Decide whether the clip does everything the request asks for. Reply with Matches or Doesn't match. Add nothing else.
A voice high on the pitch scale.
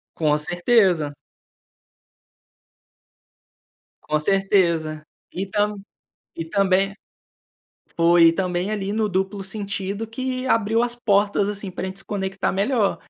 Matches